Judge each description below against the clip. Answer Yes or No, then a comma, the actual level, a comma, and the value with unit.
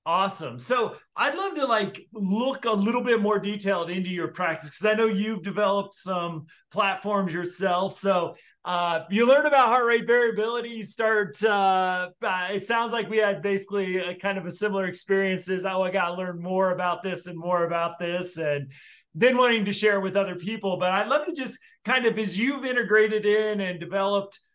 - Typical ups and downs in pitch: Yes, average, 3.4 semitones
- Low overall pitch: No, high, 200 Hz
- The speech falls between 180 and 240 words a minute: Yes, average, 200 wpm